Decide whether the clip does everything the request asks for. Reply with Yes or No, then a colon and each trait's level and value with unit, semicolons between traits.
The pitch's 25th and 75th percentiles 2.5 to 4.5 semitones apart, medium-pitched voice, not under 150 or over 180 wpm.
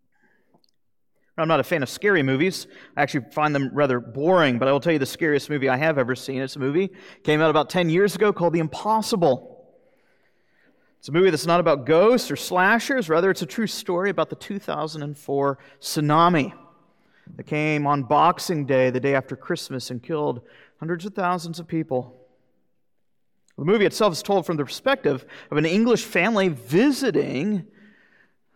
No: average, 5.2 semitones; medium, 160 Hz; average, 175 wpm